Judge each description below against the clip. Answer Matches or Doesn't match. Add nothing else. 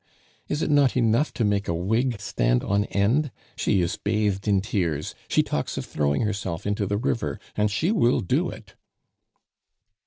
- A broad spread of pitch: Doesn't match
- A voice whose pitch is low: Matches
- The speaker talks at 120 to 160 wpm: Doesn't match